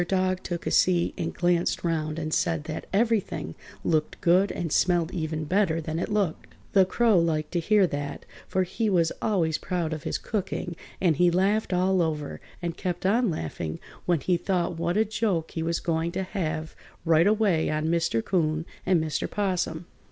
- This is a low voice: No, medium, 175 Hz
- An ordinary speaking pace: Yes, average, 185 wpm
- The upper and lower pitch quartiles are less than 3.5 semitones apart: Yes, average, 2.8 semitones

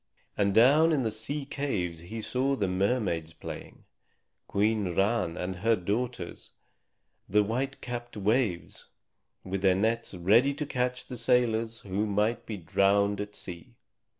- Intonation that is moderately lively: Yes, average, 4.2 semitones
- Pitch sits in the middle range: No, low, 110 Hz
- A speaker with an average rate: Yes, average, 145 wpm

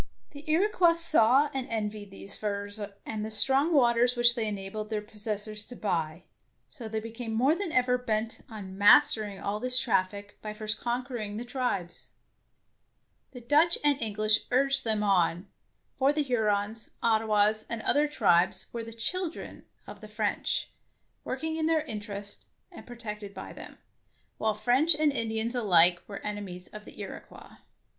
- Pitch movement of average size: Yes, average, 3.5 semitones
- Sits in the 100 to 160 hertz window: No, high, 220 Hz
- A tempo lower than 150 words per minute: No, average, 165 wpm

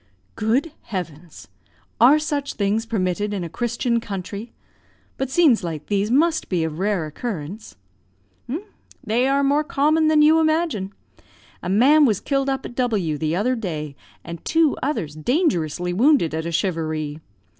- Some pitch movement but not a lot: No, wide, 8.3 semitones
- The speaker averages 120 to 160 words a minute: Yes, average, 150 wpm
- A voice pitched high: Yes, high, 215 Hz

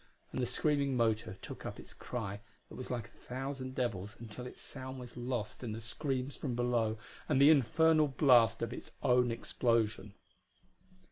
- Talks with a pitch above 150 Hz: No, low, 125 Hz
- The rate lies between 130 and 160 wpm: No, average, 175 wpm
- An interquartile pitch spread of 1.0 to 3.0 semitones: Yes, average, 2.7 semitones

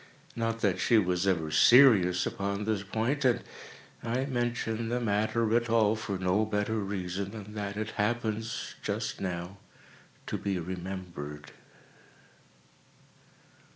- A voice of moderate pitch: No, low, 105 Hz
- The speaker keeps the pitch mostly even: No, average, 3.3 semitones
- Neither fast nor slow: No, slow, 120 wpm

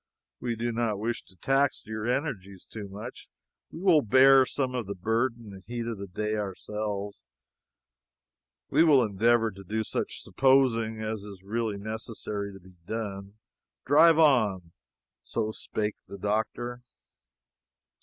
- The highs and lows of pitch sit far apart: No, average, 3.3 semitones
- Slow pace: No, average, 145 wpm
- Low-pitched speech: Yes, low, 110 Hz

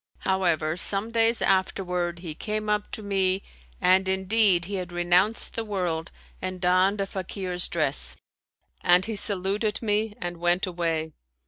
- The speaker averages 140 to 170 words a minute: Yes, average, 150 wpm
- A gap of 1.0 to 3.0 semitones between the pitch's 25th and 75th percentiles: Yes, average, 2.7 semitones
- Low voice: No, high, 190 Hz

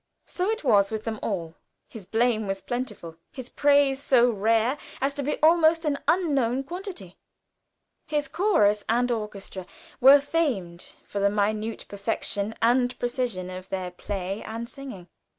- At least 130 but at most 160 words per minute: Yes, average, 150 wpm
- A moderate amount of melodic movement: No, wide, 5.7 semitones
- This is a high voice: Yes, high, 230 Hz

